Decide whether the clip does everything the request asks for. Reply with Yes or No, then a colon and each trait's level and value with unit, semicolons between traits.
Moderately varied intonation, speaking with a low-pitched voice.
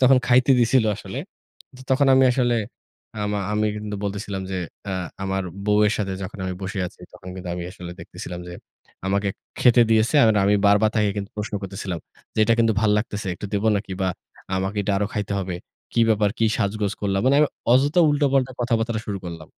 Yes: average, 3.2 semitones; low, 105 Hz